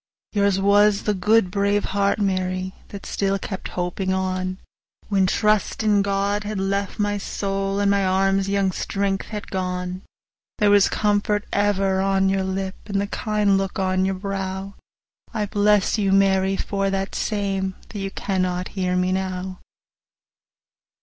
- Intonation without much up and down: Yes, narrow, 1.3 semitones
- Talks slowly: No, average, 160 wpm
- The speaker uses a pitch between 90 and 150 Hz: No, high, 195 Hz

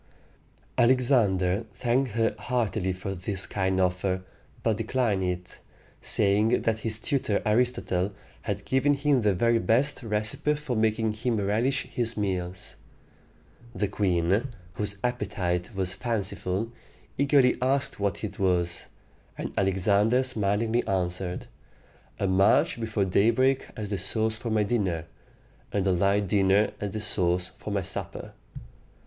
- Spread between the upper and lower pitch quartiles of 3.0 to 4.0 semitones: Yes, average, 3.7 semitones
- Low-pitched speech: Yes, low, 105 Hz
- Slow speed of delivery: Yes, slow, 130 wpm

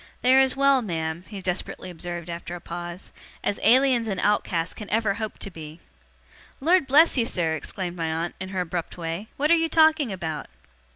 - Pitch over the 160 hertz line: Yes, high, 190 Hz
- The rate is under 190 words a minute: No, average, 195 wpm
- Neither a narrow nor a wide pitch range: No, wide, 7.0 semitones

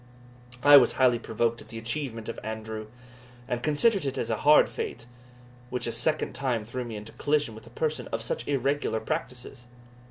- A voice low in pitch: Yes, low, 125 Hz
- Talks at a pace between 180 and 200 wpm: Yes, average, 185 wpm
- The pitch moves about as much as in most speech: Yes, average, 4.1 semitones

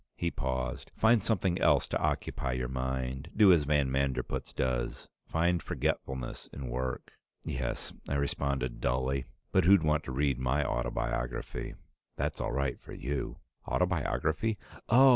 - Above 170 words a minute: No, average, 145 wpm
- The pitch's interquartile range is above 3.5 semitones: Yes, average, 4.2 semitones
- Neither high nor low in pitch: No, very low, 70 Hz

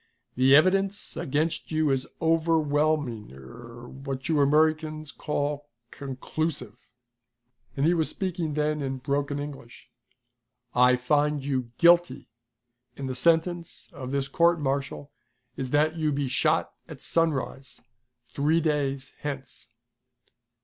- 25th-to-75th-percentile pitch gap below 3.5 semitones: Yes, average, 2.9 semitones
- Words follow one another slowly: Yes, slow, 120 wpm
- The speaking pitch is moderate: Yes, medium, 145 Hz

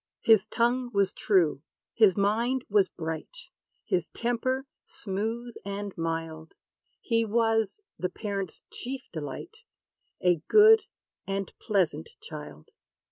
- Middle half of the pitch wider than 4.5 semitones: Yes, average, 4.9 semitones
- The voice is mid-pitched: No, high, 205 Hz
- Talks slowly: Yes, slow, 110 wpm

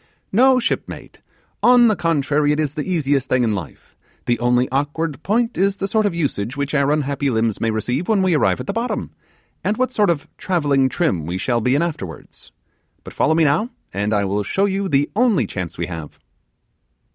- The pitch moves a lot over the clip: Yes, wide, 7.7 semitones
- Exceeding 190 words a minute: Yes, fast, 205 wpm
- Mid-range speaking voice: Yes, medium, 145 Hz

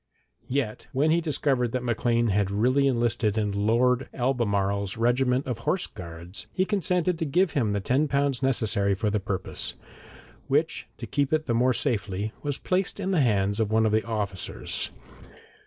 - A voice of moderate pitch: No, low, 120 Hz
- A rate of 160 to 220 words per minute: Yes, average, 170 wpm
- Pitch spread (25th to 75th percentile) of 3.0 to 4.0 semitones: No, average, 5.1 semitones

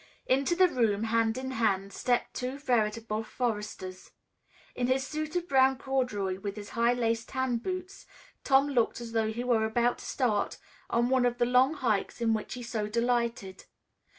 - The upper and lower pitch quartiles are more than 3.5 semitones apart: No, average, 2.9 semitones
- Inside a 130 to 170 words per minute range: No, average, 180 wpm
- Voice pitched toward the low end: No, high, 240 Hz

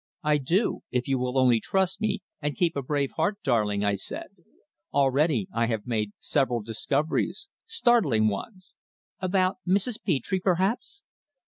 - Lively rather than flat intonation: Yes, wide, 7.9 semitones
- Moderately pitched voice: Yes, medium, 145 Hz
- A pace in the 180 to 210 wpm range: No, average, 145 wpm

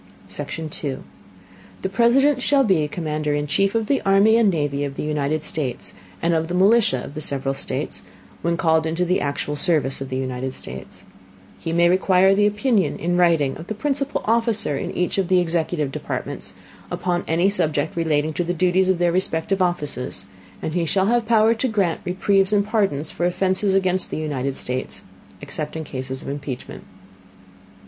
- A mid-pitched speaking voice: Yes, medium, 175 Hz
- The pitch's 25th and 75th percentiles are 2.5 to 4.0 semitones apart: No, average, 4.9 semitones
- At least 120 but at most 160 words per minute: No, average, 185 wpm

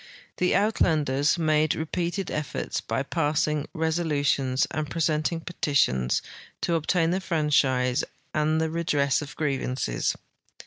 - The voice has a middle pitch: Yes, medium, 155 Hz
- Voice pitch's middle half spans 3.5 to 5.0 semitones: No, average, 2.7 semitones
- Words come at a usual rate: No, slow, 110 wpm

